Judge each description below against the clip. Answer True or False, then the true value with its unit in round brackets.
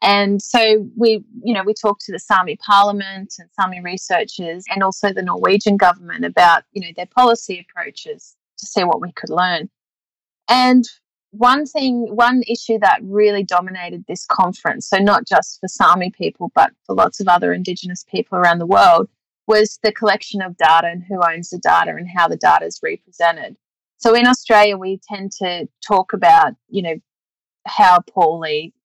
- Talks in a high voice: True (200 Hz)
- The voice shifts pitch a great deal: False (3.9 semitones)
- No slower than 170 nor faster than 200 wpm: True (175 wpm)